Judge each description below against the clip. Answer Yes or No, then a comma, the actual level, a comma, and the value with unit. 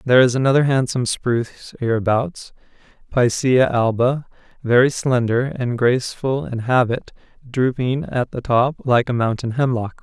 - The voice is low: Yes, low, 125 Hz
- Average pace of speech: No, slow, 130 wpm